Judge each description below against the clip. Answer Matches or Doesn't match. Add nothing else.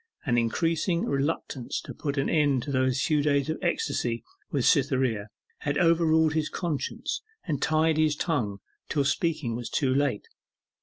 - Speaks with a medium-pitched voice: Matches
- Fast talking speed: Doesn't match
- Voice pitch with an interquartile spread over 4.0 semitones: Doesn't match